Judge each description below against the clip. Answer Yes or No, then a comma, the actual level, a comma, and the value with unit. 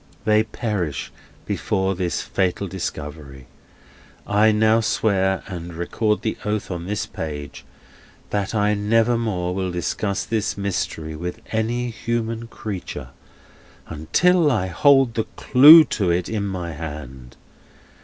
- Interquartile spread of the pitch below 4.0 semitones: No, average, 4.3 semitones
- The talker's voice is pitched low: Yes, low, 100 Hz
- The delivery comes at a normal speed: No, slow, 125 wpm